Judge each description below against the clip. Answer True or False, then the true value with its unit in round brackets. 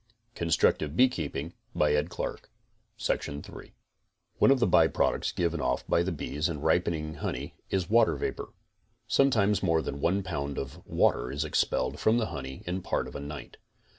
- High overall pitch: False (80 Hz)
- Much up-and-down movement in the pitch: False (4.6 semitones)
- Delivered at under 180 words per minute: True (160 wpm)